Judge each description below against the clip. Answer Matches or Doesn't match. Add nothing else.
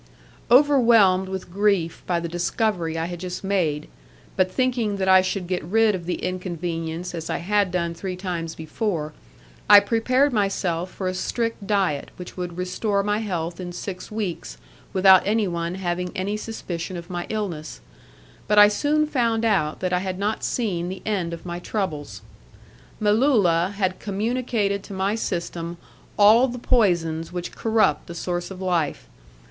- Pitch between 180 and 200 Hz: Matches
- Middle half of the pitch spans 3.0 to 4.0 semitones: Matches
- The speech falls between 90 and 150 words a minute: Doesn't match